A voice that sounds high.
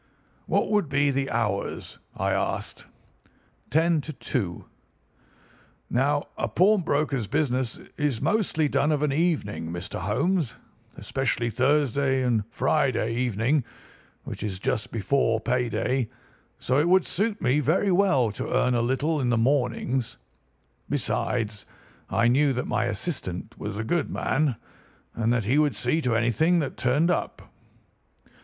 No: low, 130 Hz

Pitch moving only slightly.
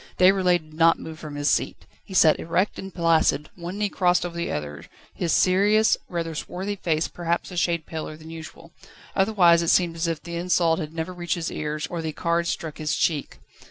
Yes: narrow, 2.1 semitones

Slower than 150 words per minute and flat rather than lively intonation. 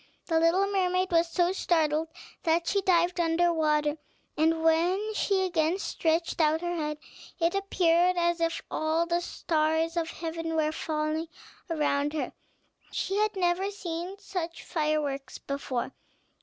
Yes: average, 140 wpm; narrow, 2.1 semitones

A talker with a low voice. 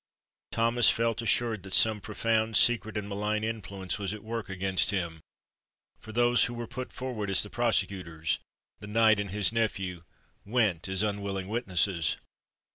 Yes: low, 105 Hz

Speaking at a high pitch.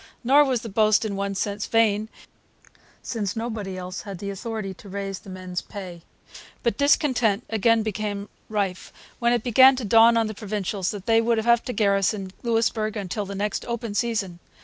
Yes: high, 215 Hz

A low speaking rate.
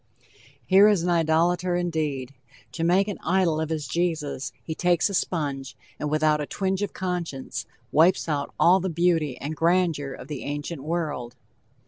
No: average, 165 wpm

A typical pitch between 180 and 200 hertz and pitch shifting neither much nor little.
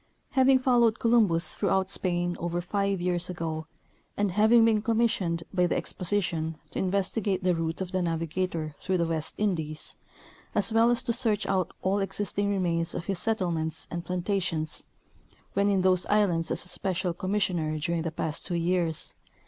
Yes: medium, 185 Hz; average, 3.4 semitones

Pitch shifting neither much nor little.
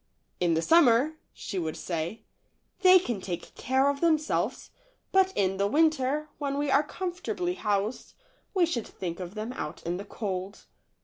No: wide, 8.4 semitones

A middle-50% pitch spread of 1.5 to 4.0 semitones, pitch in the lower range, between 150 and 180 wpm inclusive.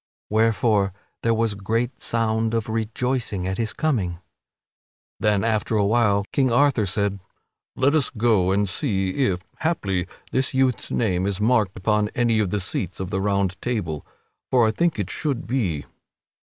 Yes: average, 3.6 semitones; low, 110 Hz; average, 165 wpm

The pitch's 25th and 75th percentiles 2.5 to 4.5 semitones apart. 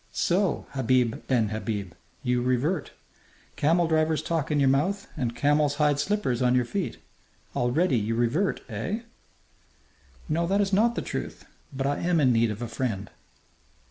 No: wide, 5.6 semitones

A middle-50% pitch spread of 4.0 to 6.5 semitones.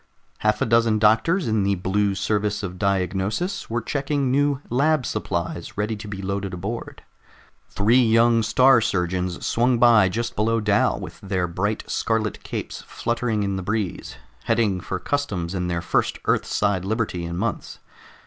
No: average, 3.6 semitones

